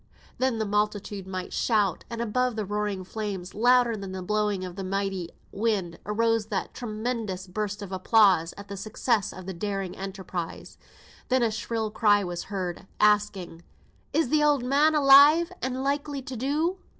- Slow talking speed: No, average, 165 wpm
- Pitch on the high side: Yes, high, 210 Hz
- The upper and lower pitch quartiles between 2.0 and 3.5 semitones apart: No, average, 4.1 semitones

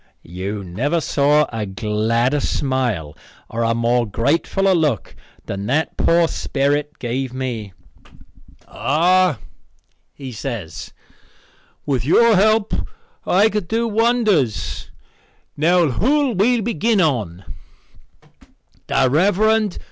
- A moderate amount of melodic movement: No, wide, 8.8 semitones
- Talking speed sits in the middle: No, slow, 105 wpm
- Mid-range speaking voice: Yes, medium, 145 Hz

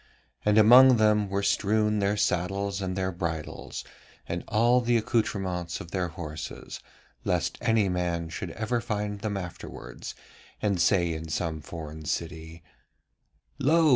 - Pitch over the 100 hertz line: No, very low, 95 Hz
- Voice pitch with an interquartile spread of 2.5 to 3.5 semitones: No, average, 4.1 semitones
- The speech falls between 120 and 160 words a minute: Yes, average, 140 wpm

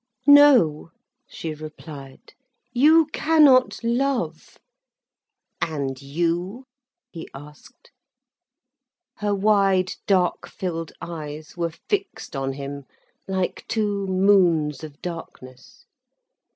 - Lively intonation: Yes, wide, 5.7 semitones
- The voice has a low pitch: No, medium, 175 Hz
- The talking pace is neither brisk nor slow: No, slow, 85 wpm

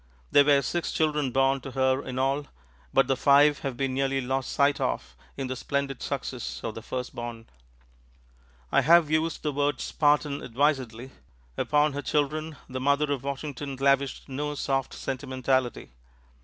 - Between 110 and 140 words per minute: No, average, 155 wpm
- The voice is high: No, low, 135 Hz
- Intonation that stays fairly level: Yes, narrow, 1.9 semitones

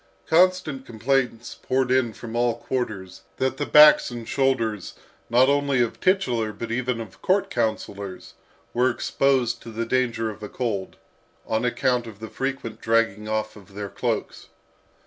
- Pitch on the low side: Yes, low, 120 Hz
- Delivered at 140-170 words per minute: Yes, average, 155 wpm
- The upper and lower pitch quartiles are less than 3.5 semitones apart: Yes, average, 3.1 semitones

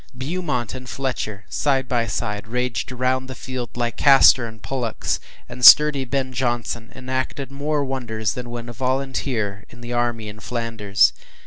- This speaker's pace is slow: No, average, 155 wpm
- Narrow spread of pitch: Yes, narrow, 2.3 semitones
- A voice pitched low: Yes, low, 125 Hz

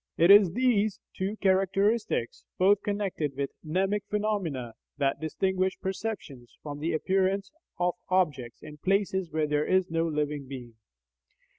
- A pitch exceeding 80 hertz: Yes, medium, 185 Hz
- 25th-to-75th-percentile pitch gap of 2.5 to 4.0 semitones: No, average, 4.8 semitones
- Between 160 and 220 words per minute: No, slow, 135 wpm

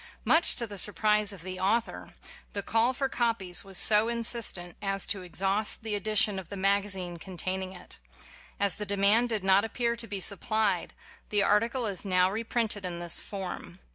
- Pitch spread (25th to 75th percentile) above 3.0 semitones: No, average, 2.7 semitones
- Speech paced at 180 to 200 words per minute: Yes, average, 185 wpm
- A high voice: Yes, high, 200 Hz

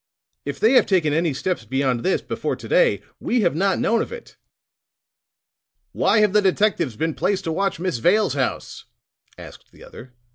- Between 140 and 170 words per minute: No, average, 180 wpm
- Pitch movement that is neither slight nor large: No, wide, 6.8 semitones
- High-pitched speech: No, medium, 180 Hz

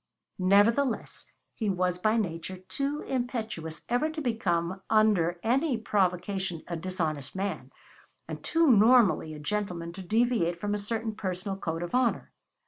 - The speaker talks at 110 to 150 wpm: Yes, average, 140 wpm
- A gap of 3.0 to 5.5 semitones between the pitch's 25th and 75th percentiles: Yes, average, 4.8 semitones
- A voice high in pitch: Yes, high, 200 Hz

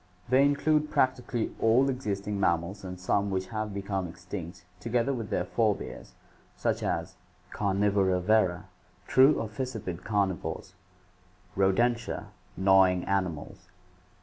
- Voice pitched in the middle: No, low, 100 Hz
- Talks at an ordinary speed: No, slow, 115 wpm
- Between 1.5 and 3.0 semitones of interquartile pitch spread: No, average, 4.0 semitones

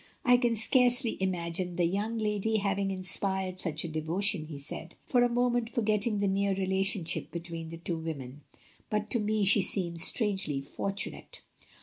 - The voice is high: Yes, high, 195 Hz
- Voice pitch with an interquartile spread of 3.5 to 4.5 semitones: Yes, average, 4.1 semitones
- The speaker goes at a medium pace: Yes, average, 160 wpm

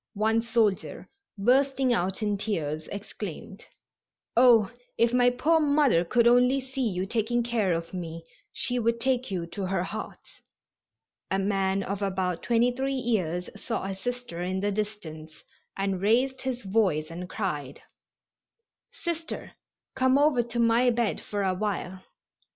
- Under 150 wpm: Yes, average, 140 wpm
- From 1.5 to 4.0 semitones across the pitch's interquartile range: No, average, 4.6 semitones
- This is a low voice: No, high, 215 Hz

